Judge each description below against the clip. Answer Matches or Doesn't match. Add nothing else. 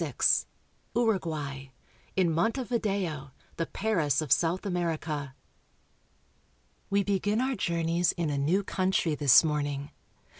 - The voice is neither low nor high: Matches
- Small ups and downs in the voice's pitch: Doesn't match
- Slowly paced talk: Matches